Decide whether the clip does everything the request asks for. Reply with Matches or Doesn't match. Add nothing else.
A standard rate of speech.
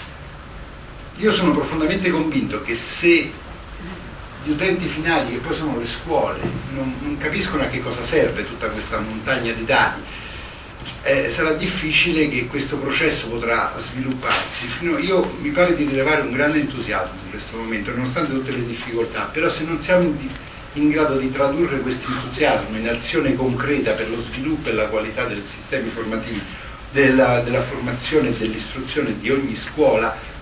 Matches